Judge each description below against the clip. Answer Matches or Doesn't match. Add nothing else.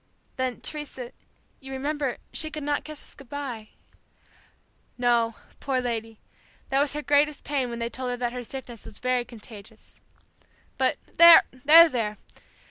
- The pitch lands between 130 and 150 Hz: Doesn't match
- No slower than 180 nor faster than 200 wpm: Doesn't match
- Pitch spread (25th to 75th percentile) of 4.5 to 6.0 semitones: Doesn't match